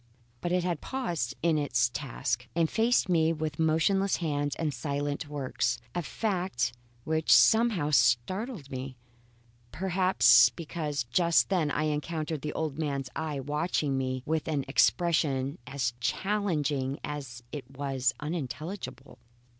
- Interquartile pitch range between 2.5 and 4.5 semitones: Yes, average, 4.1 semitones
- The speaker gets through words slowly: Yes, slow, 130 wpm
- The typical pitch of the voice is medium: Yes, medium, 150 Hz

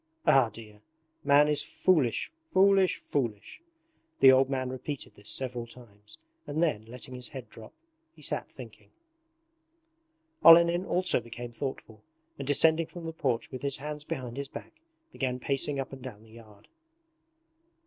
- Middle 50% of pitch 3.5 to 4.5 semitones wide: Yes, average, 4.1 semitones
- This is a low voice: Yes, low, 130 Hz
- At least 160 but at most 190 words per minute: No, average, 150 wpm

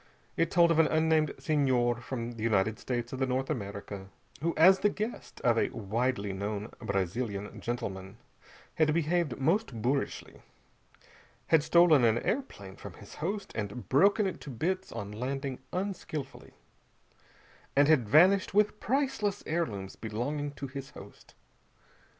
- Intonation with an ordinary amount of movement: No, wide, 6.9 semitones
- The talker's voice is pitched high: No, low, 135 Hz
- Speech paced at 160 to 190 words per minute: No, average, 145 wpm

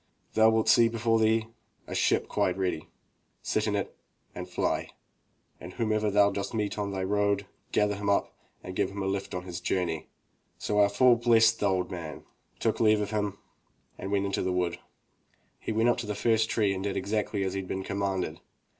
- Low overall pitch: Yes, low, 100 Hz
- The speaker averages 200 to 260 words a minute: Yes, fast, 205 wpm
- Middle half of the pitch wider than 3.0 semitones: No, narrow, 2.4 semitones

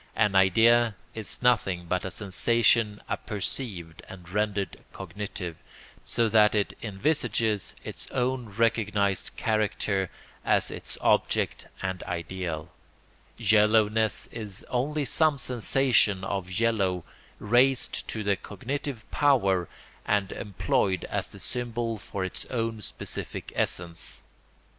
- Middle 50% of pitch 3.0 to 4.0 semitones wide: Yes, average, 3.6 semitones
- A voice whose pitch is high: No, low, 105 Hz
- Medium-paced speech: No, slow, 110 wpm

